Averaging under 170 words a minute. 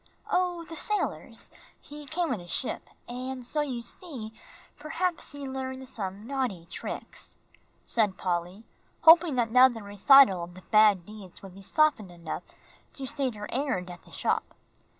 Yes: average, 160 wpm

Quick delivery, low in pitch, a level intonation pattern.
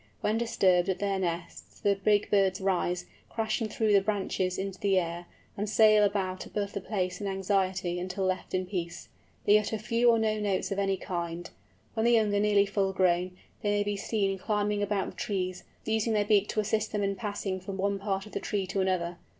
No: fast, 210 wpm; high, 200 Hz; narrow, 2.0 semitones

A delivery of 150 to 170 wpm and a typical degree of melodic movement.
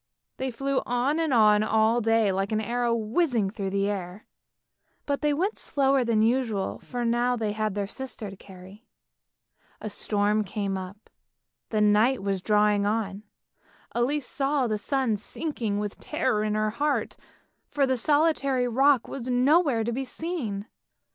Yes: average, 160 wpm; average, 4.2 semitones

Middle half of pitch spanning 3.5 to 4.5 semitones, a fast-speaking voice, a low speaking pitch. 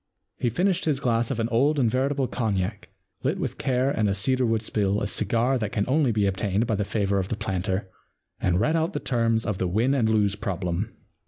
Yes: average, 4.2 semitones; fast, 225 wpm; low, 110 Hz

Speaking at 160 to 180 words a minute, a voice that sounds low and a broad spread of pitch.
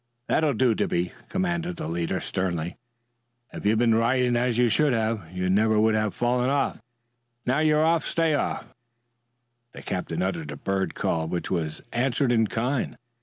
Yes: average, 170 wpm; low, 115 Hz; wide, 6.1 semitones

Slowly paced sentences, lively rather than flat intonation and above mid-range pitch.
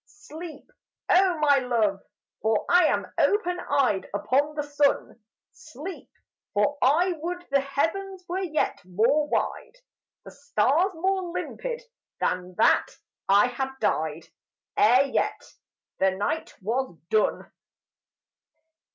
Yes: slow, 115 wpm; wide, 7.9 semitones; very high, 285 Hz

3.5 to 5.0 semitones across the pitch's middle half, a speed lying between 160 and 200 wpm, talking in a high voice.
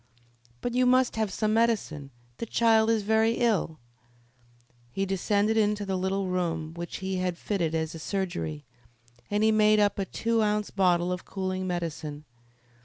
Yes: average, 3.8 semitones; average, 165 wpm; high, 195 Hz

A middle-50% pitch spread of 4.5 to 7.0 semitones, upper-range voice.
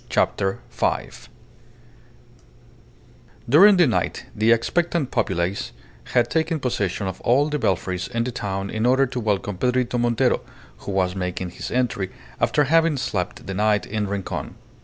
No: average, 5.0 semitones; low, 115 Hz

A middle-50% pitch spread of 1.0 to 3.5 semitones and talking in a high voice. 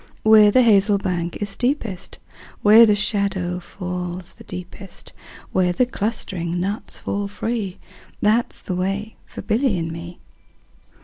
Yes: average, 3.1 semitones; high, 200 Hz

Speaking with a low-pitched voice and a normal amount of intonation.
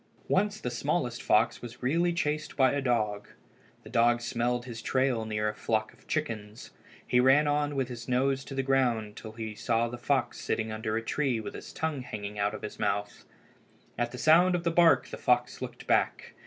Yes: low, 125 Hz; average, 4.2 semitones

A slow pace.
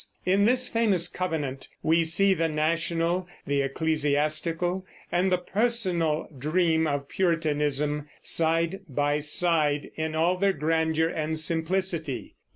Yes: slow, 120 wpm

